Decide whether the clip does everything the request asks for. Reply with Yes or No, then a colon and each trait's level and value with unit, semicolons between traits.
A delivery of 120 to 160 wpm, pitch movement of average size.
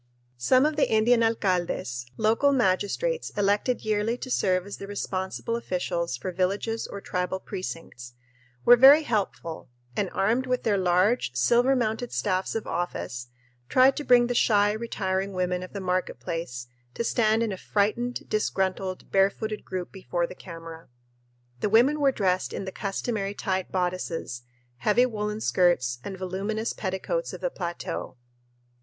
Yes: average, 150 wpm; average, 4.1 semitones